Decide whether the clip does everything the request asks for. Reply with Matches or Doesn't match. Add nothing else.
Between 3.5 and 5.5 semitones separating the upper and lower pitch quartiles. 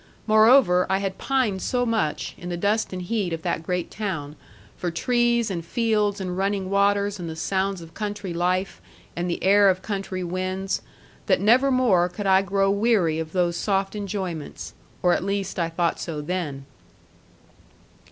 Doesn't match